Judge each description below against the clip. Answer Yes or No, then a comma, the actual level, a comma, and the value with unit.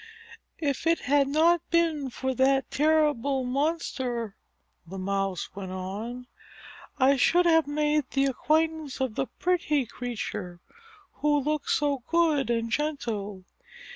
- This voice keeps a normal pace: No, slow, 125 wpm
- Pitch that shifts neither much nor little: Yes, average, 4.5 semitones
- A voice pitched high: Yes, very high, 275 Hz